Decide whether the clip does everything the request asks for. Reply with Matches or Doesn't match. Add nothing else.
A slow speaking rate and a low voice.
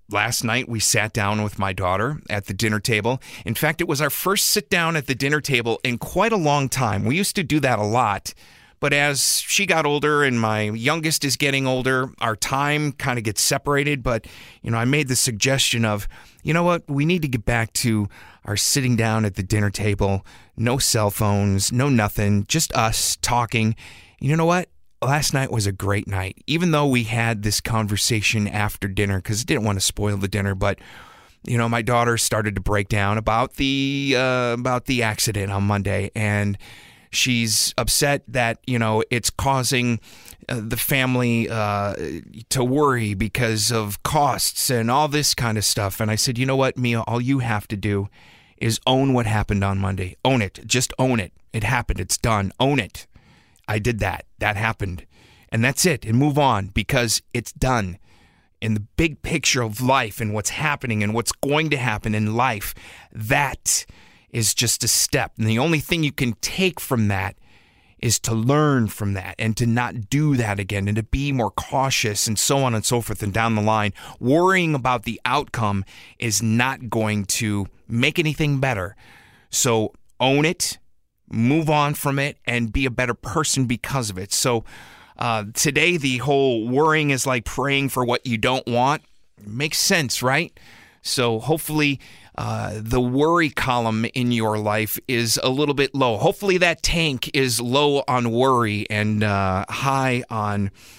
Doesn't match